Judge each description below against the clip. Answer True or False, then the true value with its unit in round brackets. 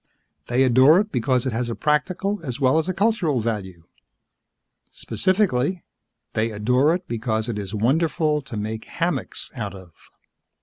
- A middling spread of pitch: False (6.5 semitones)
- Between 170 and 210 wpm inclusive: False (150 wpm)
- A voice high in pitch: False (130 Hz)